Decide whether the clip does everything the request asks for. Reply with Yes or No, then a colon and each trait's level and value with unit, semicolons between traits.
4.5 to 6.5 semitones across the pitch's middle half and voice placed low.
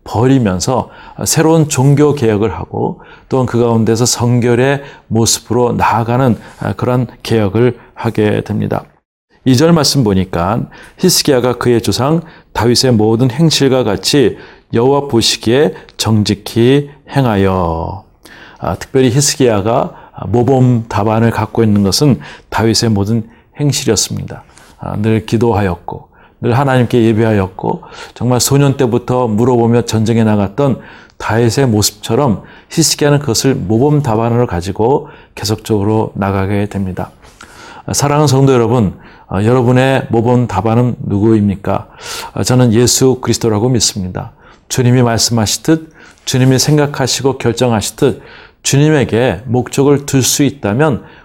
No: average, 3.2 semitones; low, 120 Hz